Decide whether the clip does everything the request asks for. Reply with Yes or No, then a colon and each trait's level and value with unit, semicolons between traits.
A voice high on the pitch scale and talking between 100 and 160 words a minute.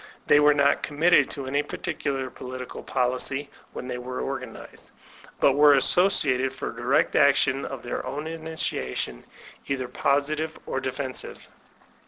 No: low, 135 Hz; average, 140 wpm